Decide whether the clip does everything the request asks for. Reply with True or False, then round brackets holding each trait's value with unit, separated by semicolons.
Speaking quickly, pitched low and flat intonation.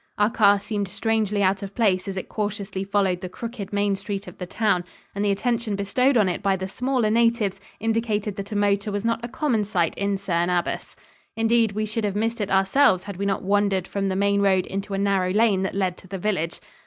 False (230 wpm; 200 Hz; 2.0 semitones)